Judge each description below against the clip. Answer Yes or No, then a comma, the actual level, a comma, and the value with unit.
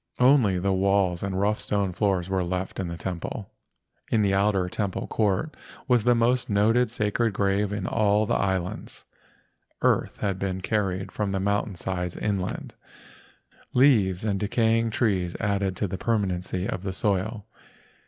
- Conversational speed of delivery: Yes, average, 155 wpm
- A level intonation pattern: Yes, narrow, 2.2 semitones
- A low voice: Yes, low, 100 Hz